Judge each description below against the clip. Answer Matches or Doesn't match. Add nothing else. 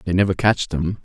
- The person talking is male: Matches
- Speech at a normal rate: Doesn't match